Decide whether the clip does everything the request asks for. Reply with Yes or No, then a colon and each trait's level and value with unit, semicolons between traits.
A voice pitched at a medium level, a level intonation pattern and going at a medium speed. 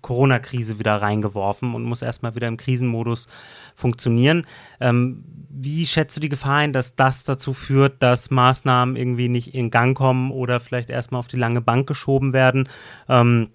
No: low, 125 Hz; narrow, 2.1 semitones; average, 170 wpm